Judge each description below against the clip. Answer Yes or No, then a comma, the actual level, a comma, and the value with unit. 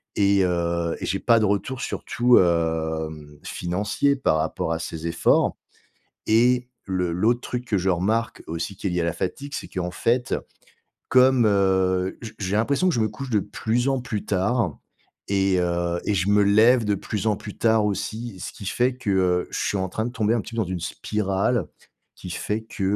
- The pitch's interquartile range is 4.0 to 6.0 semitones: Yes, average, 4.4 semitones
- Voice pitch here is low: Yes, low, 100 Hz